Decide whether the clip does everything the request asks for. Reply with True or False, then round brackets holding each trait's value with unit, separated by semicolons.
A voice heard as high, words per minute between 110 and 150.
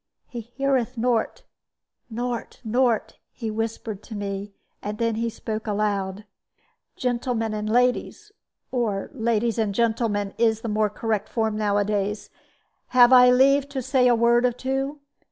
True (230 Hz; 135 wpm)